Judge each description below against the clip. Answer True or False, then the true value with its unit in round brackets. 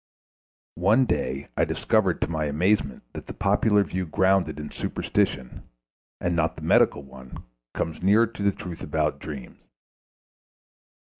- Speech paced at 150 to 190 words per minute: False (140 wpm)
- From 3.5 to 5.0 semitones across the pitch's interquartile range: False (5.4 semitones)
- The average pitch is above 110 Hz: False (85 Hz)